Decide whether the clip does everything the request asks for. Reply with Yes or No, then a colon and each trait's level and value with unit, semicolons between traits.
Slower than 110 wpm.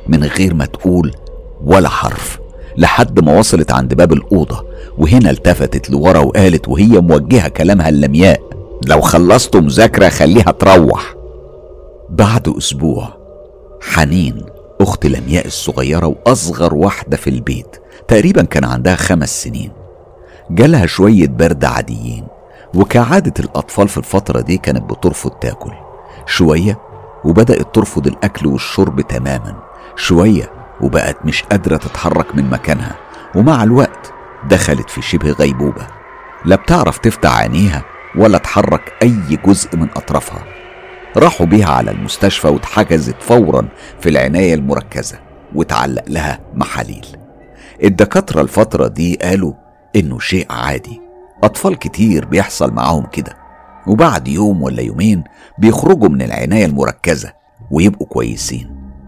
No: average, 115 wpm